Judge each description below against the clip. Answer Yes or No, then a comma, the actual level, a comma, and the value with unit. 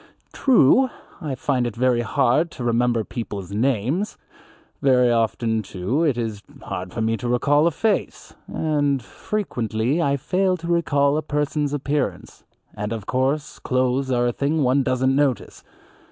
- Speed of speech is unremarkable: Yes, average, 155 wpm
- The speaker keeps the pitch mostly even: No, average, 3.8 semitones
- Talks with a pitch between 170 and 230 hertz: No, low, 130 Hz